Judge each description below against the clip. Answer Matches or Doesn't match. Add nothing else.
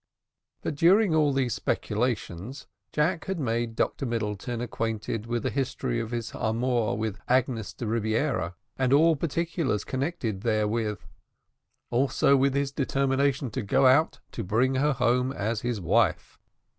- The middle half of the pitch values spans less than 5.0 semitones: Matches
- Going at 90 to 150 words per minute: Matches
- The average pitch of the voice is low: Matches